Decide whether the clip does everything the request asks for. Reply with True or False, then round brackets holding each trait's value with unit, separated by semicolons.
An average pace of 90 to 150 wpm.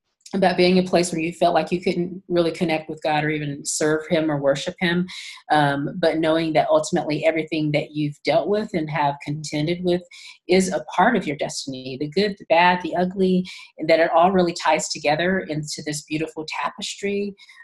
False (200 wpm)